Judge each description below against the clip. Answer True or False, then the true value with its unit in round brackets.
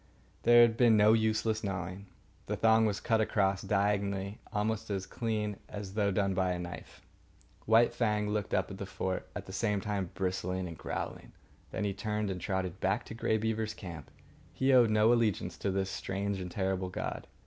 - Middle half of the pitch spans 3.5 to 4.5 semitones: False (2.5 semitones)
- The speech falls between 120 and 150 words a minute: False (190 wpm)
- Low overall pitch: True (100 Hz)